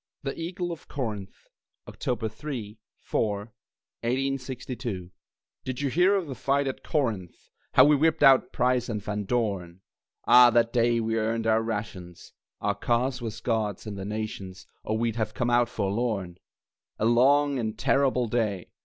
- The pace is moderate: Yes, average, 155 wpm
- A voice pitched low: Yes, low, 115 Hz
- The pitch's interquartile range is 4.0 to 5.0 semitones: No, average, 3.6 semitones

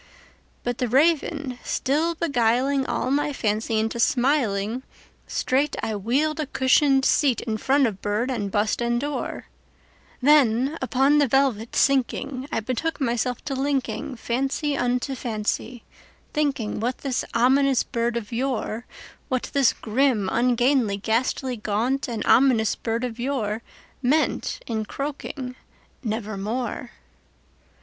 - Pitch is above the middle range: Yes, very high, 250 Hz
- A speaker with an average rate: No, slow, 115 wpm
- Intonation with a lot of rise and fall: No, average, 3.5 semitones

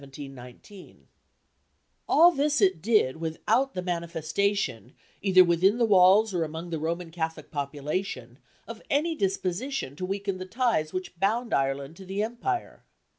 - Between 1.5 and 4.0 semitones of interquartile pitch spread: No, average, 5.2 semitones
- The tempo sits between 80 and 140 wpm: Yes, slow, 135 wpm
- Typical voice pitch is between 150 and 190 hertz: Yes, medium, 185 Hz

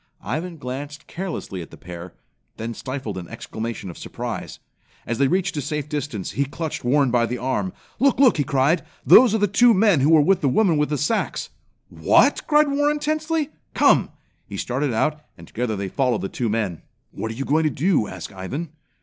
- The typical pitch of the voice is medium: Yes, medium, 145 Hz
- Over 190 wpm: Yes, average, 200 wpm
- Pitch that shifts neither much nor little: No, wide, 7.6 semitones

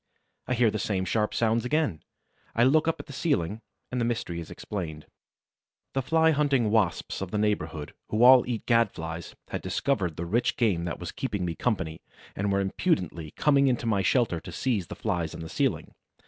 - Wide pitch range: Yes, wide, 6.3 semitones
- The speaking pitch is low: Yes, low, 105 Hz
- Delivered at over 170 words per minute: Yes, average, 200 wpm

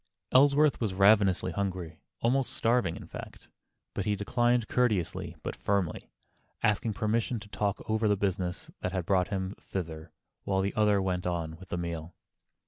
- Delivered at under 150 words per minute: No, average, 160 wpm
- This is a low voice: Yes, low, 100 Hz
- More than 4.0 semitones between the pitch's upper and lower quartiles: No, average, 3.3 semitones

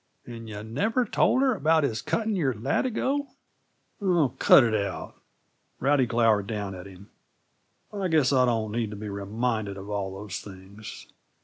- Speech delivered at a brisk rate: No, average, 170 wpm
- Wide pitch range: Yes, wide, 7.0 semitones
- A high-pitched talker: No, low, 115 Hz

